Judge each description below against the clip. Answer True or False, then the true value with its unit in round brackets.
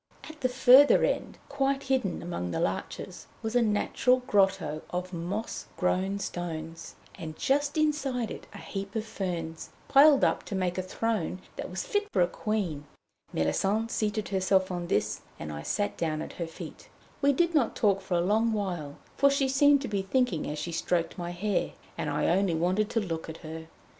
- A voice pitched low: False (195 Hz)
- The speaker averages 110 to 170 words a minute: False (190 wpm)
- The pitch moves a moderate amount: False (6.3 semitones)